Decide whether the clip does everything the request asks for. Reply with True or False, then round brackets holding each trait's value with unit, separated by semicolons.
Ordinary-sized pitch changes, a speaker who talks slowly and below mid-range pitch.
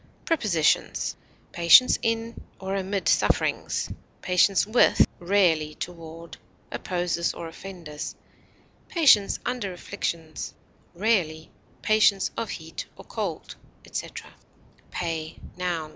False (3.8 semitones; 95 wpm; 180 Hz)